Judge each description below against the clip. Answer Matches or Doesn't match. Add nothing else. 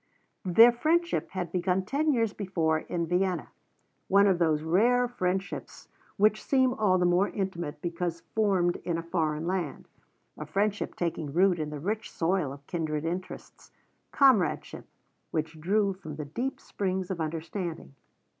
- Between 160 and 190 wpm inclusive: Doesn't match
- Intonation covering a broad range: Doesn't match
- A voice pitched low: Doesn't match